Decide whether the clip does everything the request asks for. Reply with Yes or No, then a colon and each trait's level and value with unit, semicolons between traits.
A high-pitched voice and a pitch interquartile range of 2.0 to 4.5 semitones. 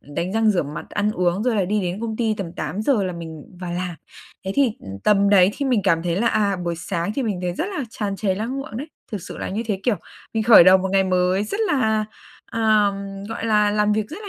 Yes: high, 205 Hz; average, 3.4 semitones